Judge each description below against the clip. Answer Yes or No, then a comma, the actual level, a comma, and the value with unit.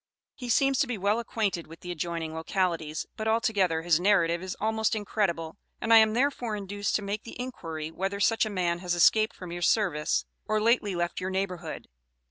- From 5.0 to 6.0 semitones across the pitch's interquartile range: No, average, 4.2 semitones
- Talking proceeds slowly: No, average, 195 wpm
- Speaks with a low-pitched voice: No, high, 195 Hz